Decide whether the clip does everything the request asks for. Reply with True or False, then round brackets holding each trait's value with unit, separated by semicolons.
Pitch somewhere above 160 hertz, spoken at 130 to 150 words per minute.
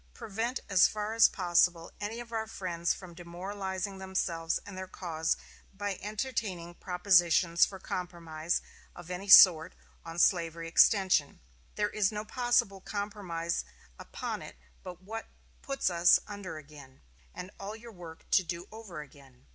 True (185 Hz; 145 wpm)